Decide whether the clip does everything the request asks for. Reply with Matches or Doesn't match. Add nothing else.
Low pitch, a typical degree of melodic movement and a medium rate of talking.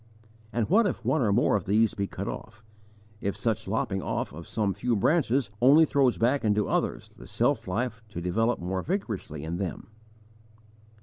Matches